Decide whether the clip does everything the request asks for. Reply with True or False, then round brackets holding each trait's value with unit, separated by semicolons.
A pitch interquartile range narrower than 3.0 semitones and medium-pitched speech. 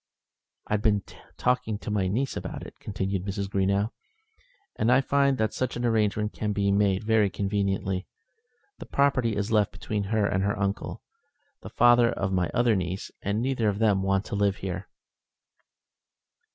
False (2.5 semitones; 105 Hz)